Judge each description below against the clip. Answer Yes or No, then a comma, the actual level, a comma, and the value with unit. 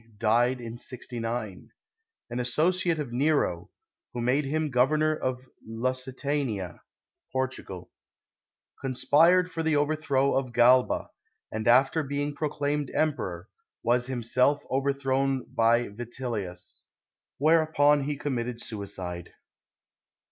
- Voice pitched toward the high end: No, low, 130 Hz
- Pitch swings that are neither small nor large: Yes, average, 3.6 semitones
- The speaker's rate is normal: No, slow, 105 wpm